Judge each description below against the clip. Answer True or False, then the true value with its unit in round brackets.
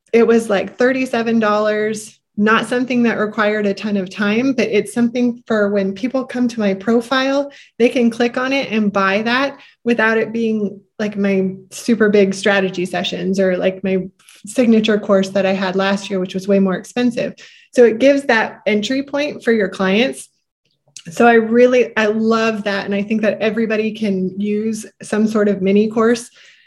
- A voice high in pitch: True (215 Hz)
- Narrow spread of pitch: False (3.2 semitones)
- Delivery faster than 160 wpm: True (180 wpm)